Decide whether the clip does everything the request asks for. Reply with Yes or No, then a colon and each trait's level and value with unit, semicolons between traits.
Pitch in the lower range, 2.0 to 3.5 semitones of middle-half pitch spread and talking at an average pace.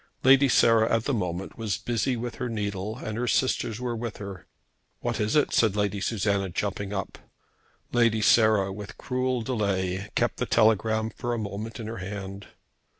Yes: low, 110 Hz; average, 2.8 semitones; average, 175 wpm